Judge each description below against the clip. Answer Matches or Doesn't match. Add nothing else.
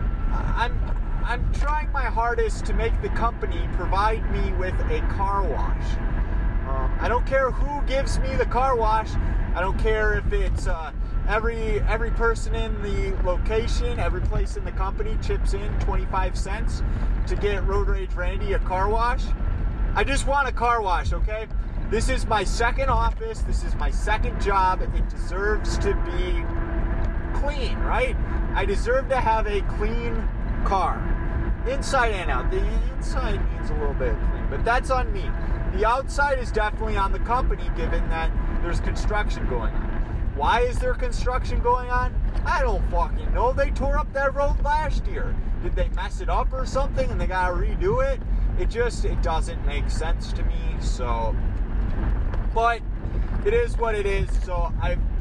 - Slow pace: Doesn't match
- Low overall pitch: Doesn't match